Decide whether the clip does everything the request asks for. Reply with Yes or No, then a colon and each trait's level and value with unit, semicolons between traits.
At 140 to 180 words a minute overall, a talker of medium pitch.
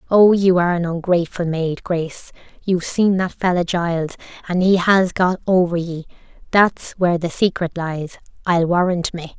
Yes: average, 165 wpm; medium, 175 Hz